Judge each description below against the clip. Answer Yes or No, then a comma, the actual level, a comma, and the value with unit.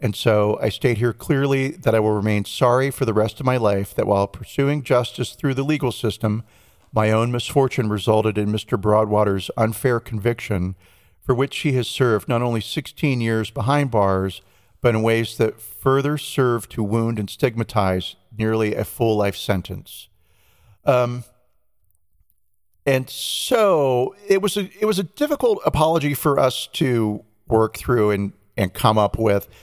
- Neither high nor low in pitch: No, low, 110 Hz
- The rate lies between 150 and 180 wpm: Yes, average, 165 wpm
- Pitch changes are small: No, average, 4.0 semitones